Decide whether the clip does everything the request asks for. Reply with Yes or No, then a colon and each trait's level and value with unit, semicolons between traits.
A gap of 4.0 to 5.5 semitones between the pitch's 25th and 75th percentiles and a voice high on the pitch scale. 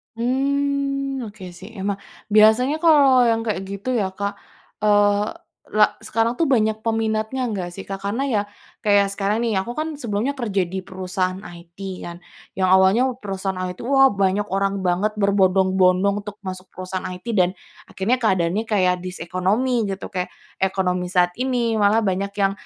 No: average, 3.4 semitones; high, 200 Hz